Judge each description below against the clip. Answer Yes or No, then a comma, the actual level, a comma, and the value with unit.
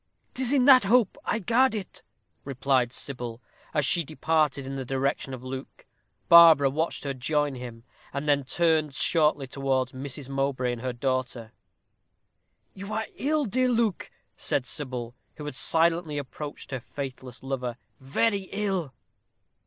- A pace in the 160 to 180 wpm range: No, average, 145 wpm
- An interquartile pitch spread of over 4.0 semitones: Yes, average, 4.6 semitones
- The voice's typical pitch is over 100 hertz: Yes, medium, 140 Hz